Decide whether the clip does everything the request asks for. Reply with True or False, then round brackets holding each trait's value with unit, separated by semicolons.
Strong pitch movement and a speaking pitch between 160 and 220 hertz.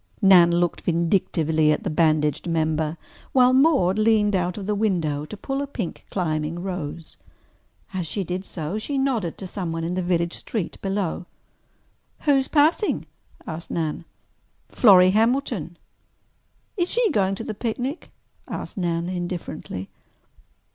False (4.7 semitones; 185 Hz)